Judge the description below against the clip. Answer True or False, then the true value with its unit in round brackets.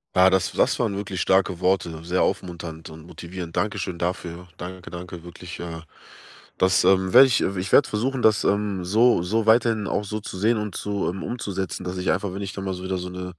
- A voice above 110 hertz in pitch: False (95 Hz)